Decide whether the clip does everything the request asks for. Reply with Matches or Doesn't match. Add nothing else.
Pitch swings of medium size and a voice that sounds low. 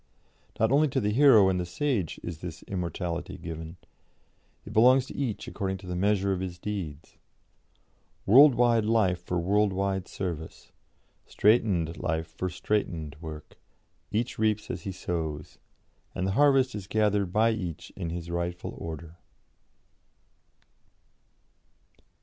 Matches